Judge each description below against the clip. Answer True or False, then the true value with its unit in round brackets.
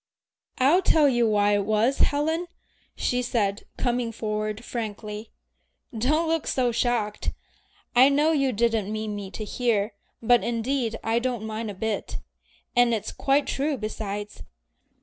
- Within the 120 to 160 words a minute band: True (145 wpm)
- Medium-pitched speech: False (230 Hz)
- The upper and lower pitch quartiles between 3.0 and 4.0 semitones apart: True (3.4 semitones)